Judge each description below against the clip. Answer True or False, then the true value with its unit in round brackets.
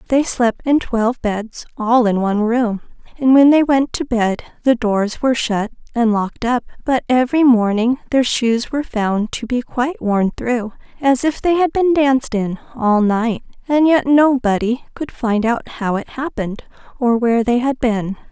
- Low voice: False (240 Hz)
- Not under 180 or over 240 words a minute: True (185 wpm)